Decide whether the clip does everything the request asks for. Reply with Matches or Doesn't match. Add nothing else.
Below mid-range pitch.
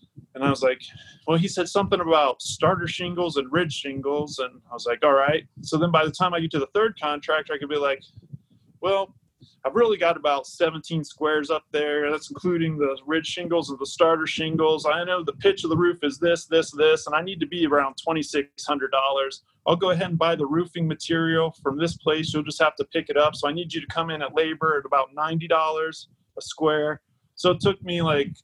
Doesn't match